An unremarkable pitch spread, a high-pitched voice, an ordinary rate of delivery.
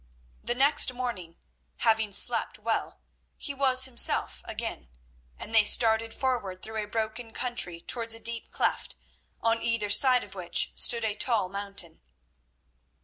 Yes: average, 3.2 semitones; high, 225 Hz; average, 145 wpm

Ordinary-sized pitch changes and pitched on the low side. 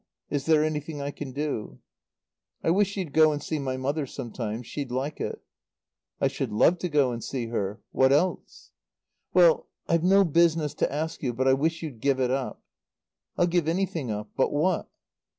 No: average, 3.8 semitones; medium, 145 Hz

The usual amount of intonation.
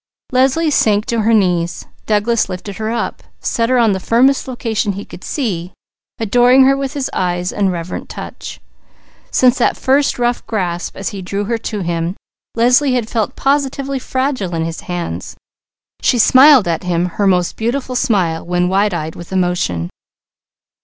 No: wide, 5.9 semitones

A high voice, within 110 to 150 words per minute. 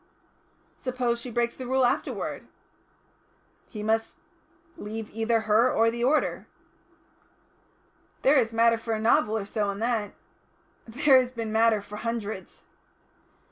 Yes: high, 230 Hz; slow, 135 wpm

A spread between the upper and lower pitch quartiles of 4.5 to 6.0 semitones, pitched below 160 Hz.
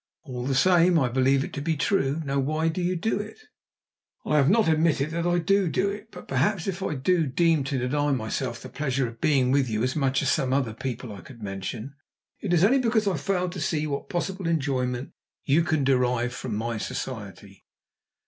Yes: average, 5.3 semitones; medium, 140 Hz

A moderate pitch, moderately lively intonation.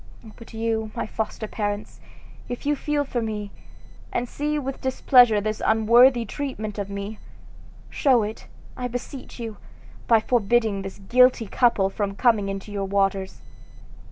No: high, 220 Hz; average, 3.3 semitones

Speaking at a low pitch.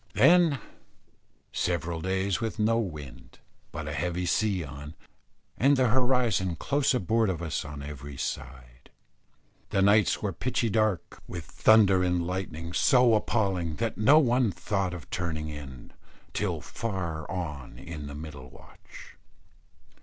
Yes: very low, 90 Hz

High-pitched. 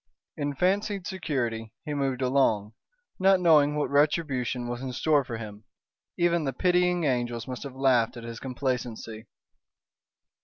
No: low, 135 Hz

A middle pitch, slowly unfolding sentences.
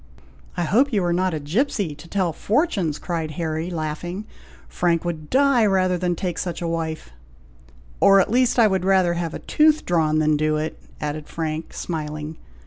No: medium, 170 Hz; average, 180 wpm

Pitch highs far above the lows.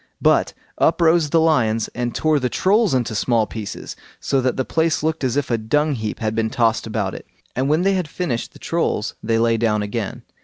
Yes: wide, 5.8 semitones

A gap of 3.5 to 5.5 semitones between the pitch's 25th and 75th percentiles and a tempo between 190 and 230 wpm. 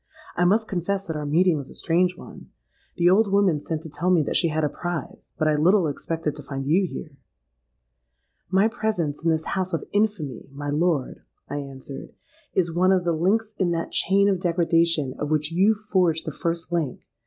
Yes: average, 3.9 semitones; average, 200 wpm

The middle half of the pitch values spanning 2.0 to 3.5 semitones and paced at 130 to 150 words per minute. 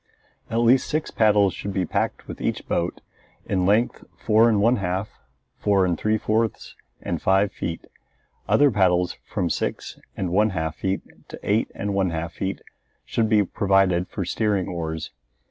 No: average, 3.1 semitones; average, 165 wpm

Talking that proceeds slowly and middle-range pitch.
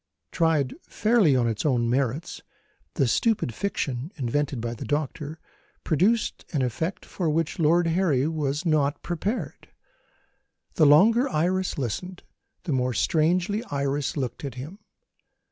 Yes: slow, 130 wpm; medium, 150 Hz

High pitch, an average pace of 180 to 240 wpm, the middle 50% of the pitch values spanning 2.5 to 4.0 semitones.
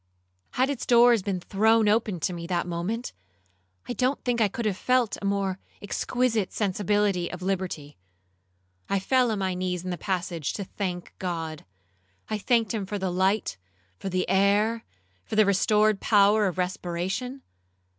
No: high, 200 Hz; average, 165 wpm; average, 3.3 semitones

